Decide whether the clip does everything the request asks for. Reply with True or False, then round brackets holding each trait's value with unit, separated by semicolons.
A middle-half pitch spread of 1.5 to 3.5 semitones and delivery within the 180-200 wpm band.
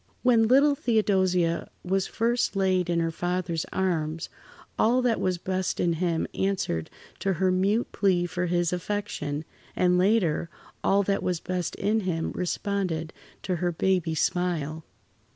False (2.8 semitones; 145 wpm)